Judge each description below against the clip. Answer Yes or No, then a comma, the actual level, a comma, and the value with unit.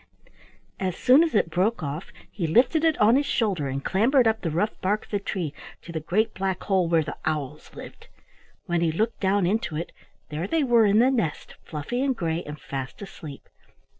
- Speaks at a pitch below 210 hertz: Yes, high, 190 Hz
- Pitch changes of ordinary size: No, wide, 5.9 semitones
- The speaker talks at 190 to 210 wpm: Yes, fast, 205 wpm